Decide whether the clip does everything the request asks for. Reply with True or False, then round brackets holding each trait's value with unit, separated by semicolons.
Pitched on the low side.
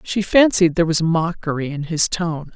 False (170 Hz)